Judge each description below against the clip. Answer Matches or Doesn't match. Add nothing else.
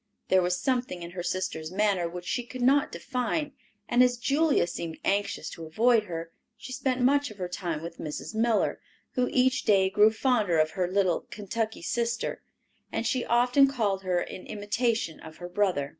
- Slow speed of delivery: Doesn't match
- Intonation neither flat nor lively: Doesn't match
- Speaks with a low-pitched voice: Doesn't match